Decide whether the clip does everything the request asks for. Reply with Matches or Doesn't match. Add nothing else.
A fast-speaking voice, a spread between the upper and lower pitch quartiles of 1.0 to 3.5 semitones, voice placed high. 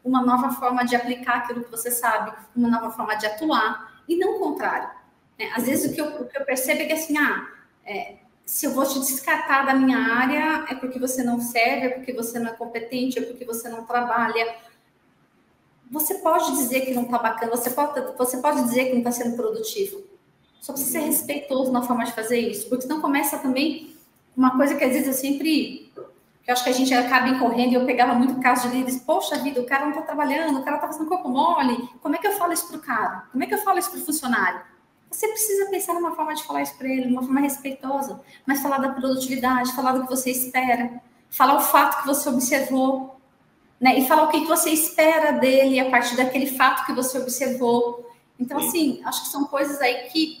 Matches